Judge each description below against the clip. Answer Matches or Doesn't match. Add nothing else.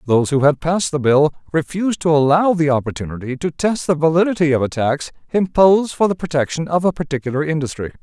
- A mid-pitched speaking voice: Matches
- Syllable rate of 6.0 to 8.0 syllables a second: Matches